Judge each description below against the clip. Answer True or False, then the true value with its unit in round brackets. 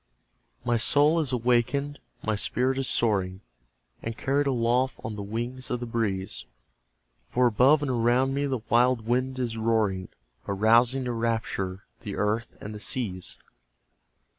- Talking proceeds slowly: False (145 wpm)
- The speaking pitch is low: True (120 Hz)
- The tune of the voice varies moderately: True (3.0 semitones)